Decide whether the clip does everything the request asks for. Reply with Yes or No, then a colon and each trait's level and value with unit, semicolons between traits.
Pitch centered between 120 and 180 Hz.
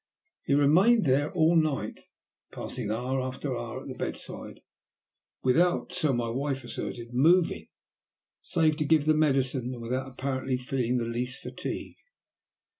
Yes: low, 135 Hz